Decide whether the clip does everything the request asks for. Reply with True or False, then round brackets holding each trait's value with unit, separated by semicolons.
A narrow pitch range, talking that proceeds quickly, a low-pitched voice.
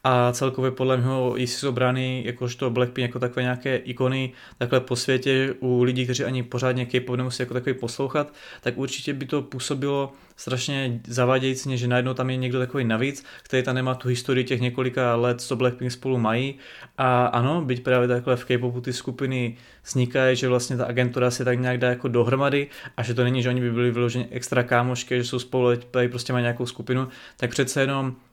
True (0.9 semitones; 195 wpm; 125 Hz)